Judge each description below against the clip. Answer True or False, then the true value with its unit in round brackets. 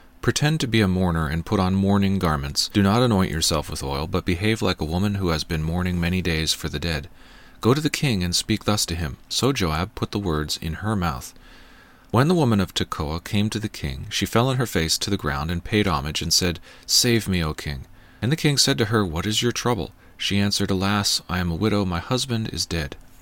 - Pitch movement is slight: False (4.7 semitones)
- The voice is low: True (95 Hz)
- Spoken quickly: True (245 wpm)